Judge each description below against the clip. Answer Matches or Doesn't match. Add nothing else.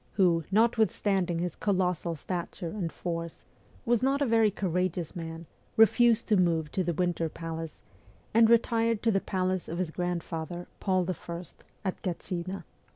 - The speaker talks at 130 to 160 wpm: Matches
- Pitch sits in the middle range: Matches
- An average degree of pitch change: Matches